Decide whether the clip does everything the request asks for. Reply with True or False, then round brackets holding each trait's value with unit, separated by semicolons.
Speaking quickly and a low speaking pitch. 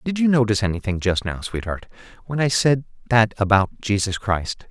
False (165 wpm; 110 Hz)